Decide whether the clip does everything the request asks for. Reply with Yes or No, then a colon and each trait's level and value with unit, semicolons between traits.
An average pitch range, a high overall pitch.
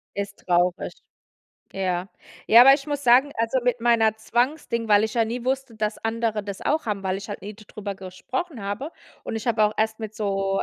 Yes: average, 3.2 semitones; high, 220 Hz